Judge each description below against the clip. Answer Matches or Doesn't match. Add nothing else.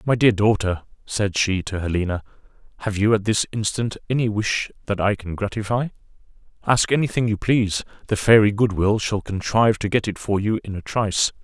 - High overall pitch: Doesn't match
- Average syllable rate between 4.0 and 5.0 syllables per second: Doesn't match